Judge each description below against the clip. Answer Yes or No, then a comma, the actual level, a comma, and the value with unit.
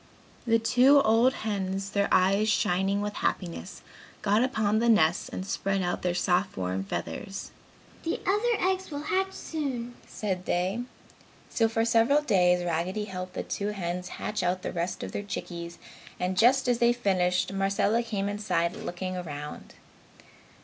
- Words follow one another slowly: No, average, 155 wpm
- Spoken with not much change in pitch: No, average, 4.2 semitones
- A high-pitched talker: Yes, high, 200 Hz